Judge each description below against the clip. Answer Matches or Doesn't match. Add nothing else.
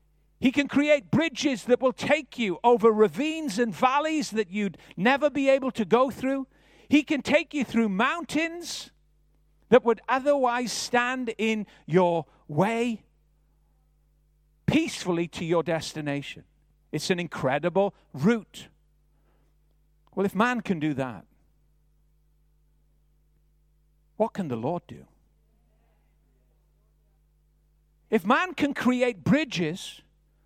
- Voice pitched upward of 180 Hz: Matches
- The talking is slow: Matches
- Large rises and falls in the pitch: Matches